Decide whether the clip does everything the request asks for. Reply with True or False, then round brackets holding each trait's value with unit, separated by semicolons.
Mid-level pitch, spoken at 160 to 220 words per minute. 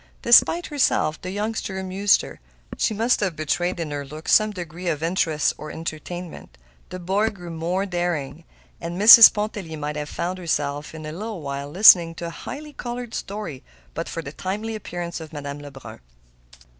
True (175 Hz; 175 wpm)